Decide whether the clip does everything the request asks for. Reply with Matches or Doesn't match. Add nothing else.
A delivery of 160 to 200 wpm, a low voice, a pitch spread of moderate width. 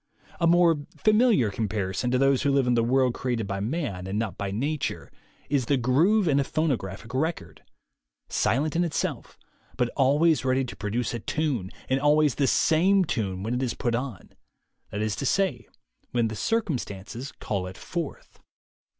Doesn't match